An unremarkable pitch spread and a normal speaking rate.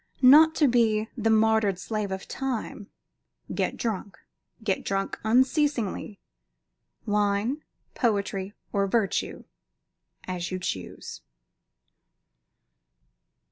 No: average, 3.3 semitones; slow, 90 wpm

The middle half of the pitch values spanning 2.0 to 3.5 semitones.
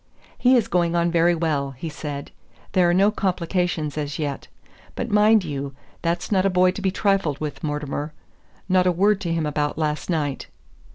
No: average, 3.9 semitones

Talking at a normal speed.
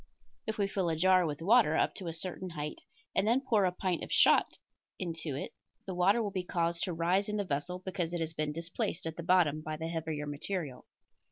No: fast, 230 wpm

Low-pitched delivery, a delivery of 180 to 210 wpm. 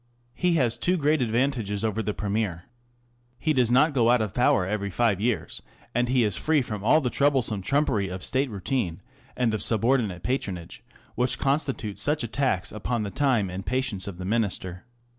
Yes: low, 115 Hz; average, 185 wpm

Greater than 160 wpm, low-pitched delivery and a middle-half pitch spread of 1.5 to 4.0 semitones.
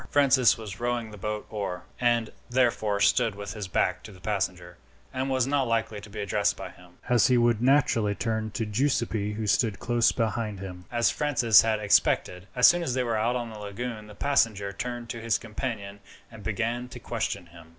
Yes: average, 200 wpm; low, 110 Hz; average, 3.0 semitones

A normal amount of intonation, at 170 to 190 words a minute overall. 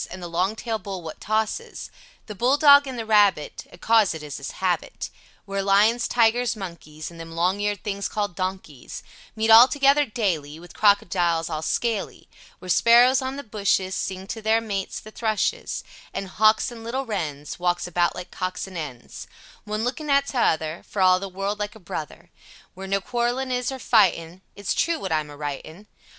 Yes: average, 4.5 semitones; average, 185 wpm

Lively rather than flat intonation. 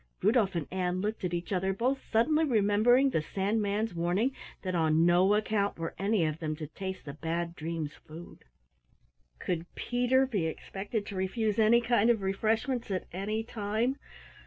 No: average, 4.4 semitones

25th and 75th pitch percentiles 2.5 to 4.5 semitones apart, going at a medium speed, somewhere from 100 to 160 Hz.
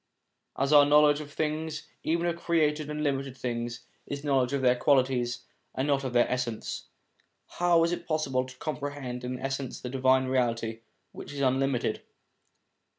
Yes: average, 3.0 semitones; average, 165 wpm; low, 135 Hz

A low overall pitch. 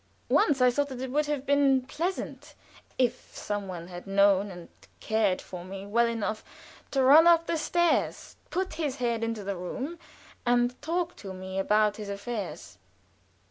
No: high, 235 Hz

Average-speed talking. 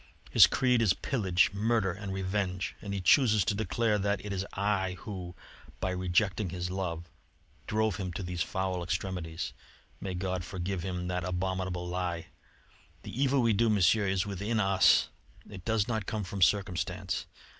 Yes: average, 165 wpm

